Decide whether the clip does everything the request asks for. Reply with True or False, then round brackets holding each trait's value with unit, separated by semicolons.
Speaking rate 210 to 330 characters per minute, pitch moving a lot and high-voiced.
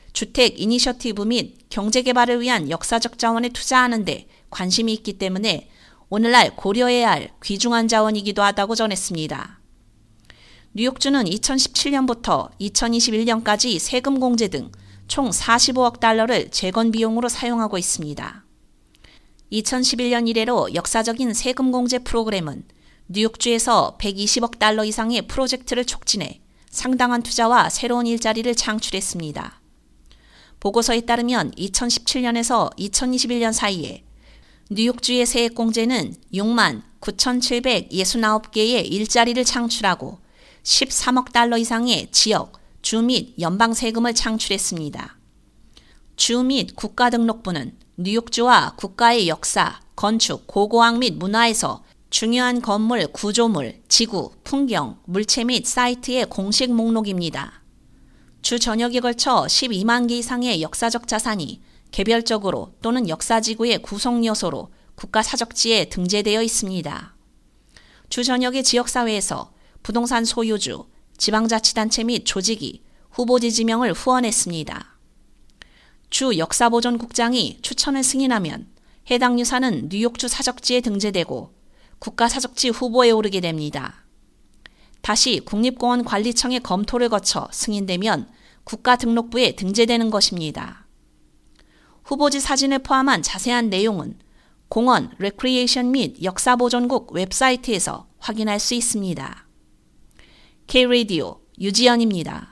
False (275 characters per minute; 2.9 semitones; 230 Hz)